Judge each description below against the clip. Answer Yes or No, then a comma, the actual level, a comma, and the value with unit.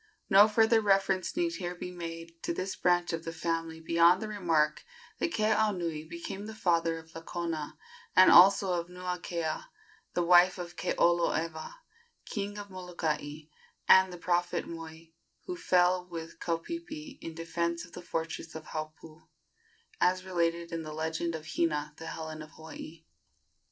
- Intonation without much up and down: Yes, narrow, 2.2 semitones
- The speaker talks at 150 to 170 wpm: Yes, average, 155 wpm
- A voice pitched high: No, medium, 170 Hz